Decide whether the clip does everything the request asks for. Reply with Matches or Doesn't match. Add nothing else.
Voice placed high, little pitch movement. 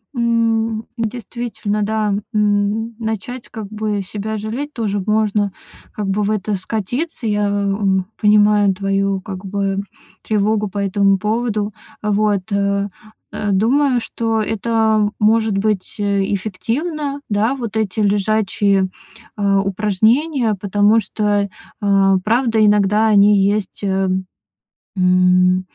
Matches